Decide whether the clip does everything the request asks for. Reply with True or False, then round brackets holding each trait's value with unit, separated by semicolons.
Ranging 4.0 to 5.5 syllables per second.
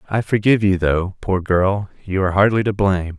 False (5.7 syllables/s)